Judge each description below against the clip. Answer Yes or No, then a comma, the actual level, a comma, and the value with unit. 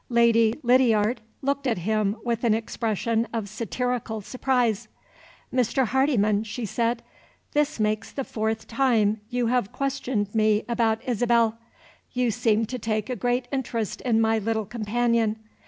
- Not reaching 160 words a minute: Yes, average, 140 wpm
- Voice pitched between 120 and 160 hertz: No, high, 230 Hz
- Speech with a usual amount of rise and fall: No, narrow, 2.2 semitones